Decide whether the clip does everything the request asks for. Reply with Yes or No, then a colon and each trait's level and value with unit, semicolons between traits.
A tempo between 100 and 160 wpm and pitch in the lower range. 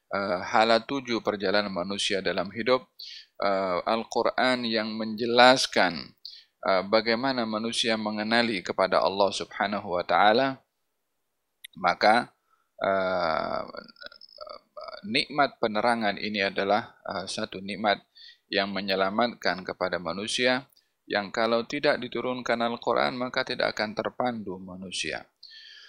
No: slow, 90 wpm; low, 115 Hz